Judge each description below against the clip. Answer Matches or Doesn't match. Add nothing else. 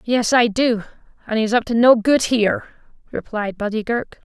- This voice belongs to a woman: Matches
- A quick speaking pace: Doesn't match